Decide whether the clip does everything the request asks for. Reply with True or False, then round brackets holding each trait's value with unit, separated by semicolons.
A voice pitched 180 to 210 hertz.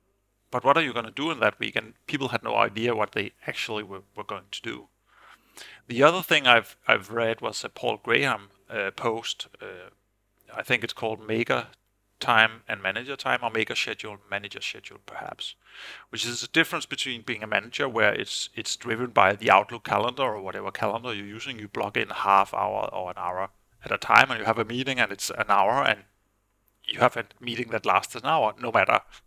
False (115 Hz)